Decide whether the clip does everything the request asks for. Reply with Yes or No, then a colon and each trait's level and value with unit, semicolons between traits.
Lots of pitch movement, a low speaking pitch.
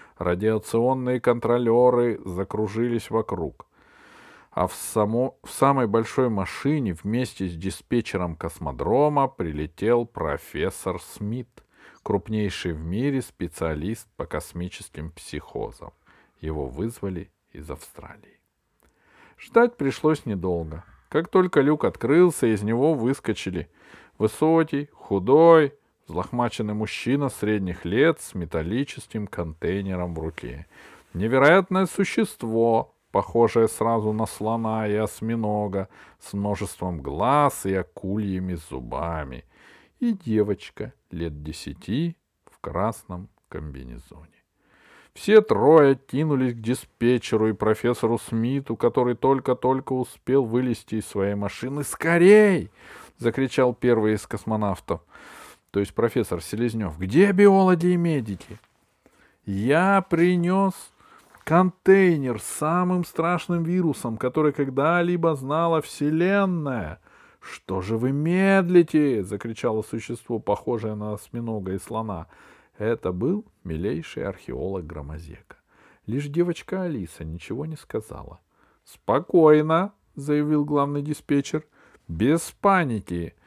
Yes: wide, 7.0 semitones; low, 115 Hz